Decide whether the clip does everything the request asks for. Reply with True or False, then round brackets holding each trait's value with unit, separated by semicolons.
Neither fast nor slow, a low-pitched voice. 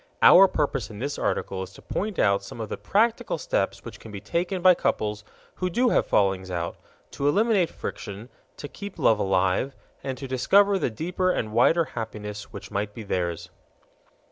True (185 wpm; 120 Hz)